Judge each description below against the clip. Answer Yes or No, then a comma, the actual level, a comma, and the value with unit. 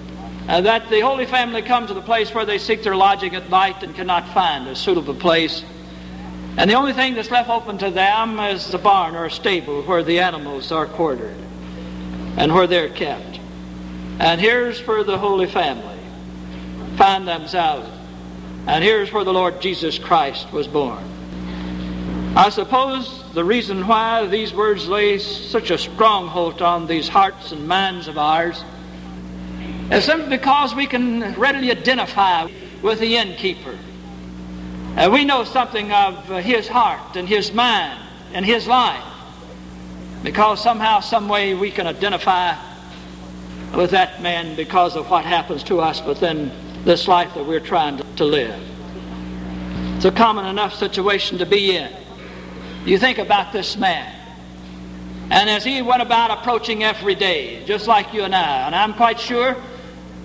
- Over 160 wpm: No, average, 155 wpm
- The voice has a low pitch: No, medium, 185 Hz